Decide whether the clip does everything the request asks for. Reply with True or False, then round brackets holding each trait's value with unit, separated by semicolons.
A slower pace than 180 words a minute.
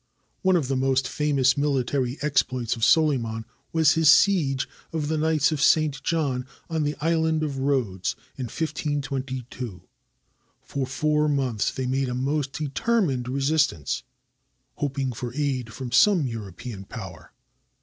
True (140 wpm)